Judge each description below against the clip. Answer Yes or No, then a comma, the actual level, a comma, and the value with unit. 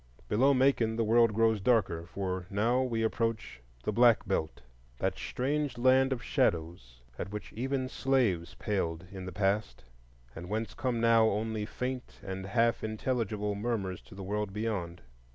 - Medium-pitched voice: No, low, 110 Hz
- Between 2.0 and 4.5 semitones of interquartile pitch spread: Yes, average, 4.0 semitones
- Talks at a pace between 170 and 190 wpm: No, average, 150 wpm